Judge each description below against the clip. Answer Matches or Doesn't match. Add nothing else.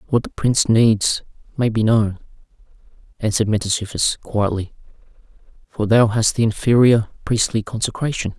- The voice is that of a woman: Doesn't match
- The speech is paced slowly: Matches